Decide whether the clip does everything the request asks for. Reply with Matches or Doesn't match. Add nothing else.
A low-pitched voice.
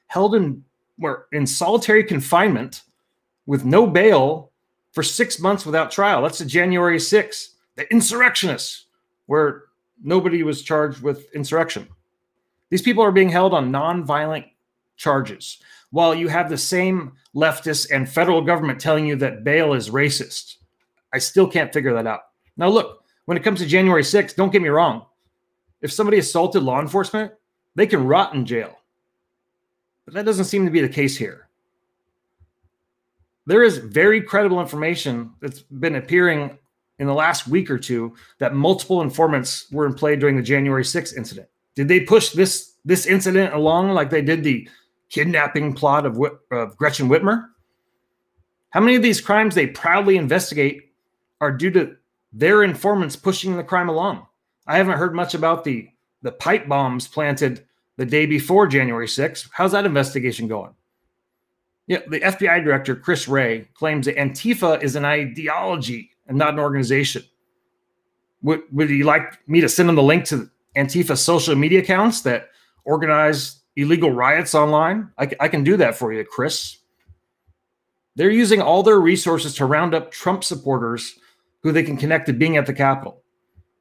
Doesn't match